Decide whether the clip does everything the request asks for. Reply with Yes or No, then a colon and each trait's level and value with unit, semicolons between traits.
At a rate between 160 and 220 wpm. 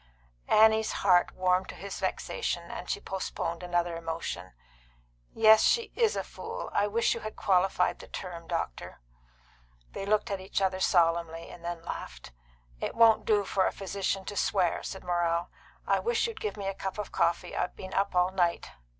Yes: average, 180 wpm